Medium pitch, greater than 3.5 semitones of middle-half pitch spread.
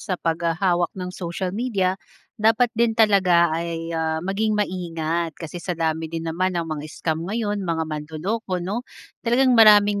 Yes: medium, 180 Hz; average, 4.0 semitones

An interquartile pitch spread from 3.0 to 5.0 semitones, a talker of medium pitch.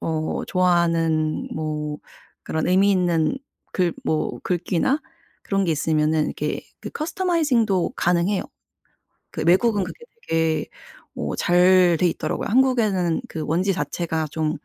Yes: average, 3.6 semitones; medium, 175 Hz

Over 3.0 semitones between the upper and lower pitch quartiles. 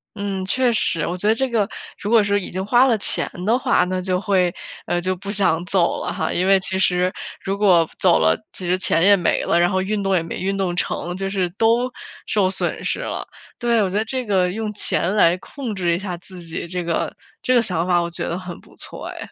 No: average, 2.7 semitones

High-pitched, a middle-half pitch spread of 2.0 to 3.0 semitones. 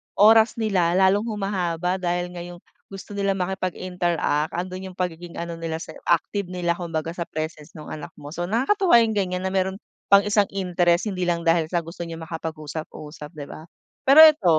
No: medium, 180 Hz; average, 2.7 semitones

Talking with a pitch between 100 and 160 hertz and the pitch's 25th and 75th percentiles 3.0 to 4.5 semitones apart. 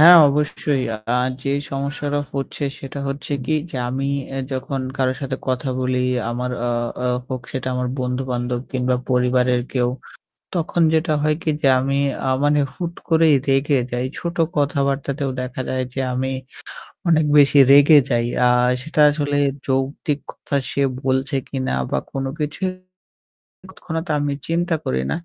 No: low, 135 Hz; narrow, 2.4 semitones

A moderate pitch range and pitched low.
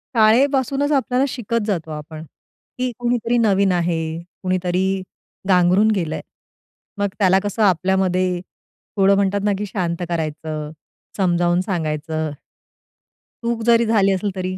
No: average, 4.0 semitones; high, 190 Hz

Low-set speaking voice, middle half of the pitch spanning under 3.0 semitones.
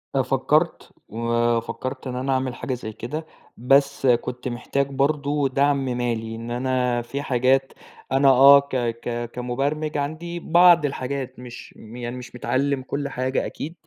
Yes: low, 130 Hz; narrow, 2.5 semitones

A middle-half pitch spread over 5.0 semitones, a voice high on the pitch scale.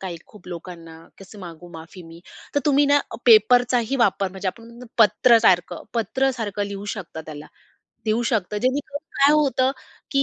Yes: wide, 5.6 semitones; high, 215 Hz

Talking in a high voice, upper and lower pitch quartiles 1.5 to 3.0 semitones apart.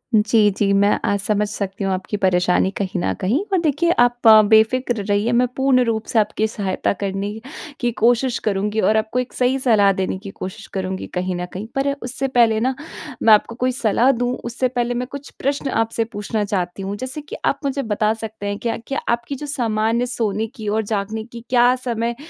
No: high, 220 Hz; average, 3.4 semitones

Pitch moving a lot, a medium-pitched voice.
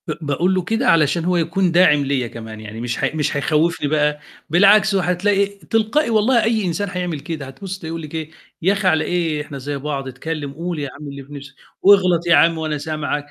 No: average, 4.1 semitones; medium, 160 Hz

